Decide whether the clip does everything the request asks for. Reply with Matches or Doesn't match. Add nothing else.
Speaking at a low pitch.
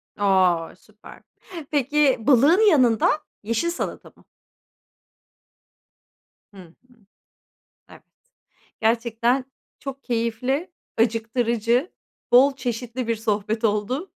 Doesn't match